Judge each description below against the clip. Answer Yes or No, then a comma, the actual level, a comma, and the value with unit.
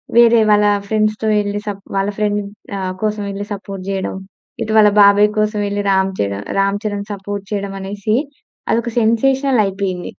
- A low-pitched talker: No, high, 205 Hz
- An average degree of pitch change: No, narrow, 1.4 semitones